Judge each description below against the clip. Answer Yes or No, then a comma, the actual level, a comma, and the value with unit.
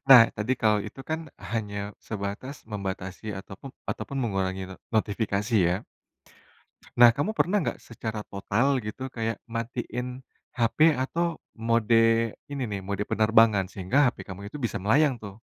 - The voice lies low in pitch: Yes, low, 110 Hz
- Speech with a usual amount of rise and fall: Yes, average, 3.6 semitones